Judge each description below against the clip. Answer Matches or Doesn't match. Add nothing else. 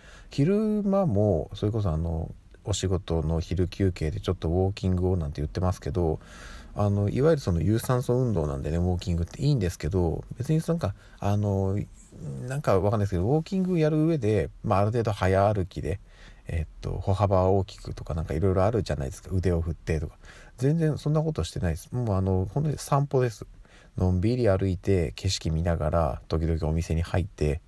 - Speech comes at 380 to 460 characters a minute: Matches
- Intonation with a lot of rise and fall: Matches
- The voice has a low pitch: Matches